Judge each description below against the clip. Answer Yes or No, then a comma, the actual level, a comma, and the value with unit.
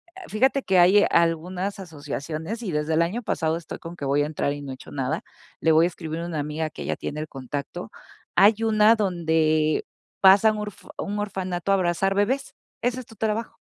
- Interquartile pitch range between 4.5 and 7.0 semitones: Yes, average, 4.8 semitones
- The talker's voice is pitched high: No, medium, 175 Hz